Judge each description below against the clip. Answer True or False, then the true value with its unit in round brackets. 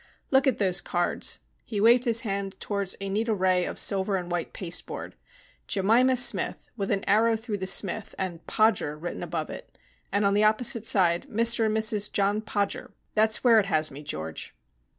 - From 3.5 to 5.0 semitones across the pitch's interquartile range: False (2.9 semitones)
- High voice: True (200 Hz)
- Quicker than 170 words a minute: True (190 wpm)